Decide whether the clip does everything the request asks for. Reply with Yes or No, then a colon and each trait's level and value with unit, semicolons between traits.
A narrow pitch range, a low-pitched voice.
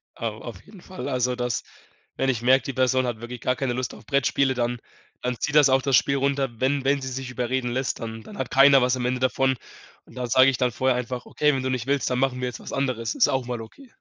Yes: narrow, 1.6 semitones; low, 130 Hz